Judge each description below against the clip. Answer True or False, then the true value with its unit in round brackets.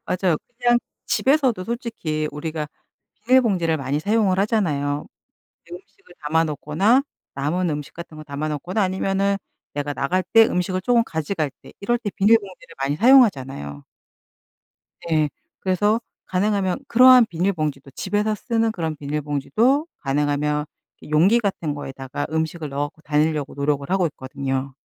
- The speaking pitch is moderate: True (165 Hz)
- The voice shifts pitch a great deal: True (5.9 semitones)